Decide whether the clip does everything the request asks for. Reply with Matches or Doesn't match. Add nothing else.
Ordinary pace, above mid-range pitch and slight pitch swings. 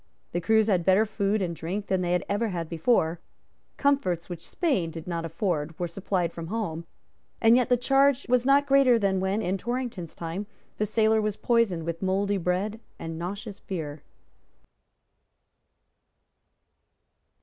Doesn't match